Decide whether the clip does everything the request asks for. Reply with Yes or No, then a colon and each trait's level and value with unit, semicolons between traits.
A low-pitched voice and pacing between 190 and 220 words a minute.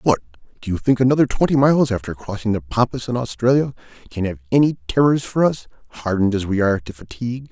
Yes: low, 115 Hz; average, 200 wpm